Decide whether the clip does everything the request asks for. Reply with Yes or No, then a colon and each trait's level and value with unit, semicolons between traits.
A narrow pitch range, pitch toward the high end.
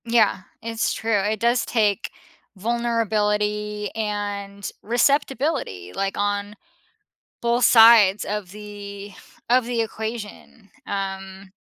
Yes: narrow, 2.3 semitones; high, 210 Hz